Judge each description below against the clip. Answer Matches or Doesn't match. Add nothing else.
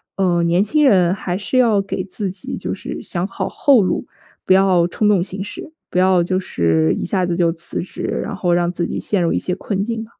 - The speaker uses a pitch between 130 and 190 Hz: Matches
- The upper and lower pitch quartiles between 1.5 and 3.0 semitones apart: Matches